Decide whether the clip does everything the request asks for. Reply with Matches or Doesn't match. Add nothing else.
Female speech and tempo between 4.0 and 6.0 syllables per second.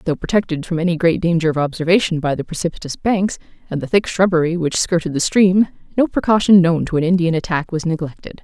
Doesn't match